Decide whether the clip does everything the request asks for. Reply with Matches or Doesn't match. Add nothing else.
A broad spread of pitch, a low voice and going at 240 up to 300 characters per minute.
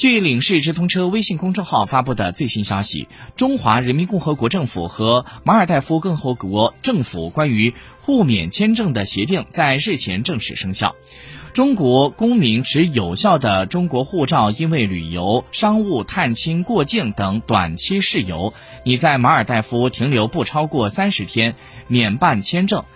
Matches